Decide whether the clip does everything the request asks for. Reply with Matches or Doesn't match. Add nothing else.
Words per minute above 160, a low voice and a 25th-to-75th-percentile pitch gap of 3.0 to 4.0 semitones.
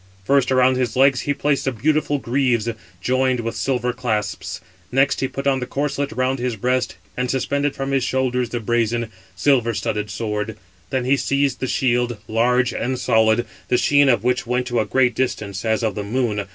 Doesn't match